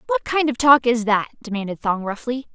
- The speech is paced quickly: Yes, fast, 210 wpm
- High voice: Yes, high, 245 Hz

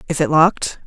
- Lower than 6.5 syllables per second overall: Yes, 6.1 syllables/s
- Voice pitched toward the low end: No, medium, 160 Hz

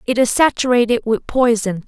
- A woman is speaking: Yes, female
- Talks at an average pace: Yes, average, 160 wpm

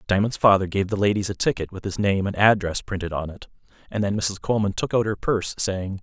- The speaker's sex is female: No, male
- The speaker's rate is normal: No, fast, 240 wpm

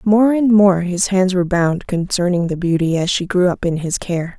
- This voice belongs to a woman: Yes, female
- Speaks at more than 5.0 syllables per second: No, 4.9 syllables/s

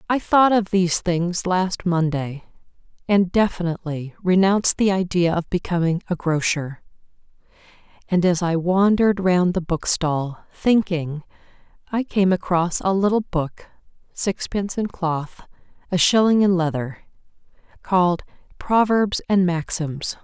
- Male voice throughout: No, female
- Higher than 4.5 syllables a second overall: No, 4.4 syllables/s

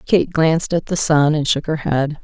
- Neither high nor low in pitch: Yes, medium, 155 Hz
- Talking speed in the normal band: No, fast, 240 wpm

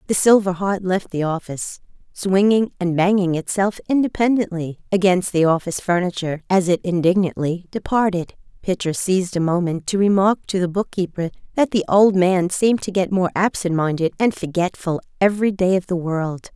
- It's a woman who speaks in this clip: Yes, female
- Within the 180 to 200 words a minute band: No, average, 165 wpm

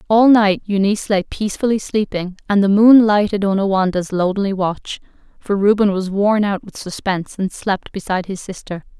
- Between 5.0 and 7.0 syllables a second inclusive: Yes, 5.3 syllables/s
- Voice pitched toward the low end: No, high, 200 Hz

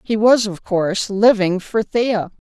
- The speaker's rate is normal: Yes, average, 170 wpm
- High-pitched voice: Yes, high, 210 Hz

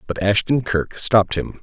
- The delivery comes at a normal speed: Yes, average, 185 wpm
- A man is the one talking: Yes, male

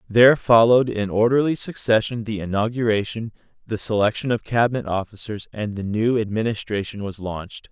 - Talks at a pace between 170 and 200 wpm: No, average, 140 wpm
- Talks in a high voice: No, low, 110 Hz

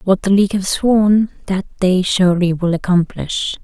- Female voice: Yes, female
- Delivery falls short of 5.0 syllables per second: Yes, 4.8 syllables/s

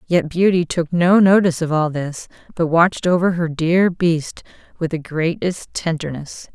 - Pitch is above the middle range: No, medium, 170 Hz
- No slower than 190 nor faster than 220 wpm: No, average, 165 wpm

